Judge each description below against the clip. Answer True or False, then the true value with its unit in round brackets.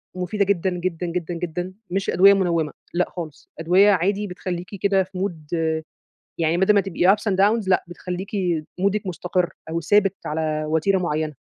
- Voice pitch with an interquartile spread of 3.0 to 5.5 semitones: False (2.6 semitones)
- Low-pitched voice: False (180 Hz)